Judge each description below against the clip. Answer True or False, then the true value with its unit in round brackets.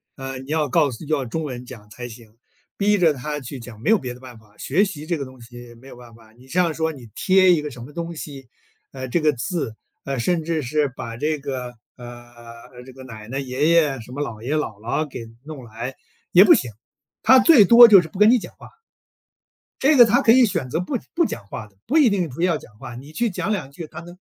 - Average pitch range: False (5.9 semitones)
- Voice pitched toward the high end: False (140 Hz)